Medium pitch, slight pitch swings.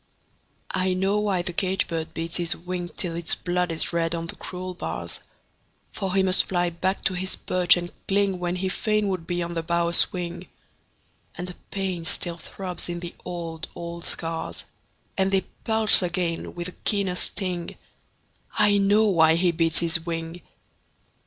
Yes: medium, 175 Hz; narrow, 1.9 semitones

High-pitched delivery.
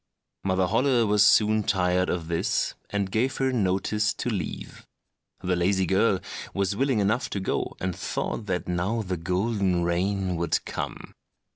No: very low, 95 Hz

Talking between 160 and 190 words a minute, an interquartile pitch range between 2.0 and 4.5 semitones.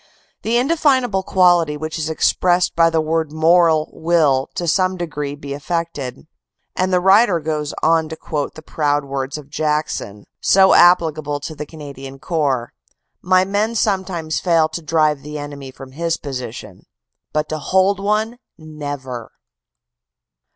No: average, 150 wpm; average, 3.5 semitones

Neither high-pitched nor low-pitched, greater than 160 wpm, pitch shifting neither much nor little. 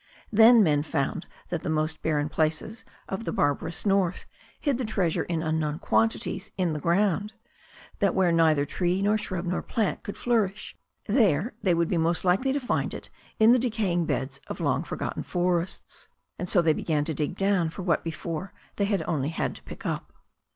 Yes: medium, 175 Hz; average, 180 wpm; average, 4.2 semitones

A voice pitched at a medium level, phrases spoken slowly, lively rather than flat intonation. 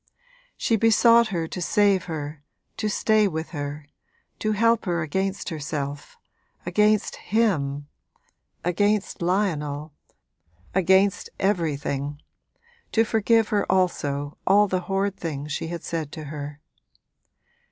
Yes: medium, 180 Hz; slow, 115 wpm; wide, 5.7 semitones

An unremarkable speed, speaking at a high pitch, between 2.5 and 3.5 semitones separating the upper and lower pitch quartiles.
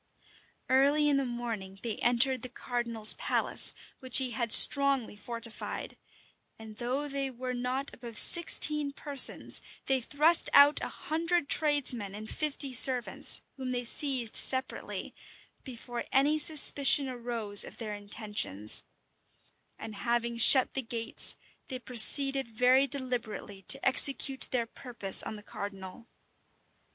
No: slow, 130 wpm; very high, 250 Hz; average, 3.2 semitones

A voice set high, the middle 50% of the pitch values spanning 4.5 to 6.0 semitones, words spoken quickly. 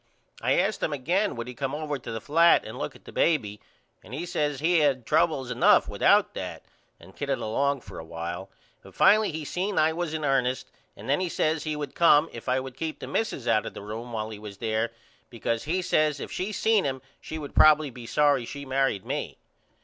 No: medium, 140 Hz; average, 5.2 semitones; fast, 225 wpm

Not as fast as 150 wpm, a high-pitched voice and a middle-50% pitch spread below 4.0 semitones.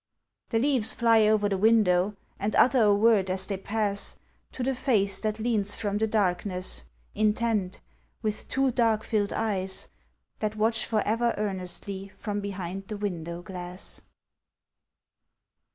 Yes: average, 140 wpm; high, 210 Hz; narrow, 2.5 semitones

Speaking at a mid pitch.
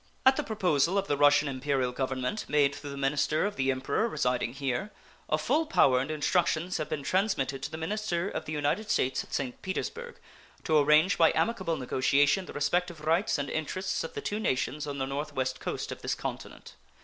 Yes: medium, 150 Hz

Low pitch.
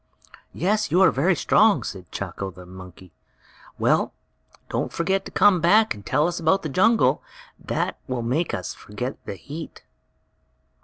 No: medium, 155 Hz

